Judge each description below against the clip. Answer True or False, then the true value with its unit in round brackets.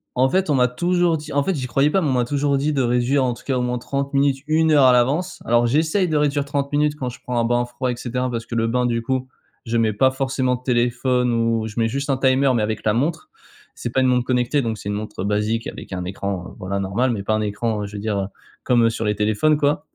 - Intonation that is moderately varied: True (3.4 semitones)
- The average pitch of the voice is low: True (125 Hz)